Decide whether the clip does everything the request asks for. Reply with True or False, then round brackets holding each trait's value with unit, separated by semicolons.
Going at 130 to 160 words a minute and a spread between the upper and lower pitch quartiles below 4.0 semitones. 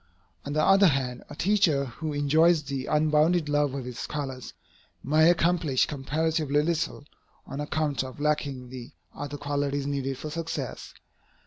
True (145 wpm; 2.5 semitones)